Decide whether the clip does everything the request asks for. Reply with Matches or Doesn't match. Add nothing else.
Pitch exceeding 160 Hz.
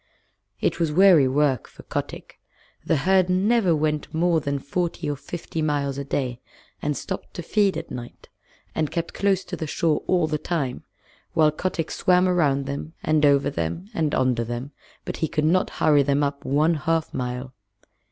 Doesn't match